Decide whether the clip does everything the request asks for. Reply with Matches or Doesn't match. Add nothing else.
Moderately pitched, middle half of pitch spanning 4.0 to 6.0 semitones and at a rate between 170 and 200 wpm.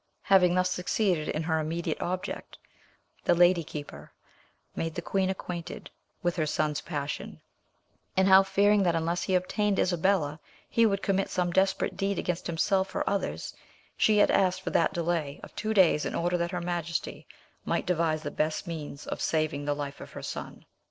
Doesn't match